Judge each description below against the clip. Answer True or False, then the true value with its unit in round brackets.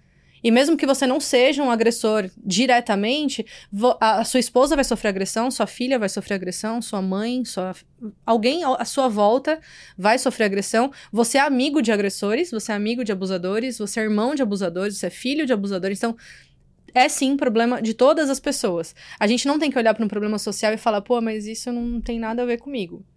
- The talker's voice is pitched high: True (230 Hz)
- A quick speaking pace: True (205 wpm)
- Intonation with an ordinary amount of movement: True (3.4 semitones)